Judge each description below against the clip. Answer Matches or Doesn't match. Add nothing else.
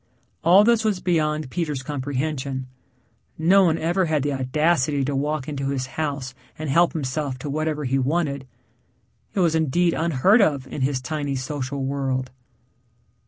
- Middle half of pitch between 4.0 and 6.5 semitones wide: Doesn't match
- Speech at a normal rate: Matches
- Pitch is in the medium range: Matches